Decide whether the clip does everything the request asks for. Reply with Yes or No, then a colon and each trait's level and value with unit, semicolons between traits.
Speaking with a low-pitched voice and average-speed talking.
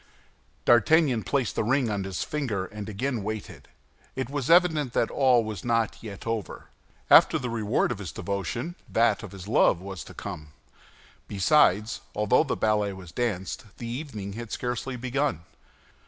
Yes: low, 115 Hz; average, 160 wpm